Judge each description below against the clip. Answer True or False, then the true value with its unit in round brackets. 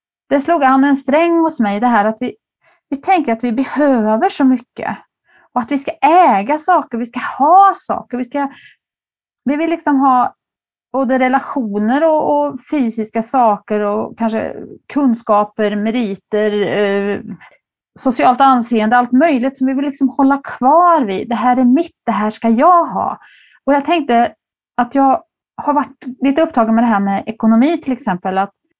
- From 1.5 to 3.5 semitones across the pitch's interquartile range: False (4.2 semitones)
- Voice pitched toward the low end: False (260 Hz)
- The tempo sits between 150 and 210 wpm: True (170 wpm)